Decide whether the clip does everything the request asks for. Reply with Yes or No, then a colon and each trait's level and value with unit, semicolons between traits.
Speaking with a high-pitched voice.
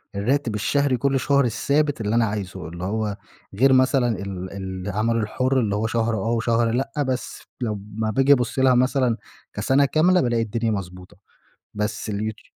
No: low, 115 Hz